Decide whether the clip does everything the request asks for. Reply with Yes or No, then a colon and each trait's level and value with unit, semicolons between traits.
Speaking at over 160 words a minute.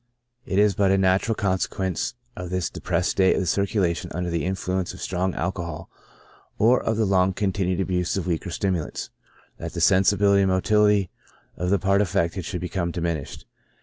Yes: average, 180 wpm